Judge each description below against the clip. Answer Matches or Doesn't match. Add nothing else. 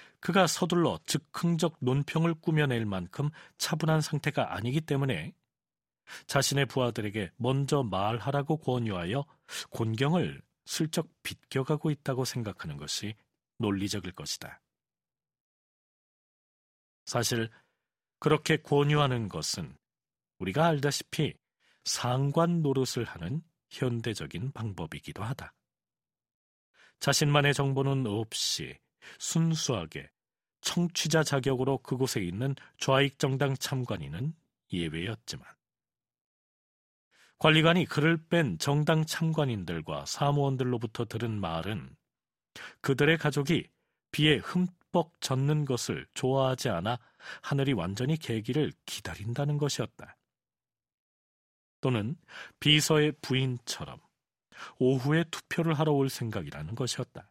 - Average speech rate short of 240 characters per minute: Doesn't match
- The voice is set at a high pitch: Doesn't match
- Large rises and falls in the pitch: Doesn't match